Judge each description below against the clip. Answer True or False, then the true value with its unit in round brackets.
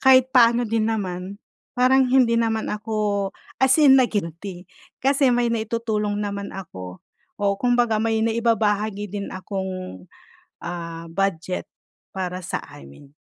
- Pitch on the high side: True (210 Hz)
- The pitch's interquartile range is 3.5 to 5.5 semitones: True (3.9 semitones)